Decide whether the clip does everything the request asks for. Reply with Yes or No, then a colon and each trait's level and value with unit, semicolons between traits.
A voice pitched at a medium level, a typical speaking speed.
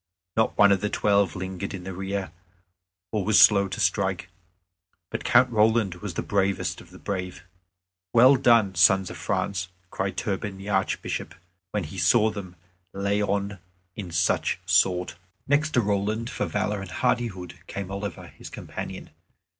No: low, 100 Hz; average, 160 wpm